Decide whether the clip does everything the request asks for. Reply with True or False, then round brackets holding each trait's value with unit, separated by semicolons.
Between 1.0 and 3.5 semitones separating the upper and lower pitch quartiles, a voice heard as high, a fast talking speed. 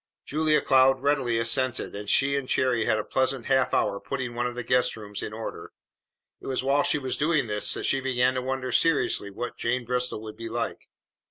False (2.5 semitones; 125 Hz; 210 wpm)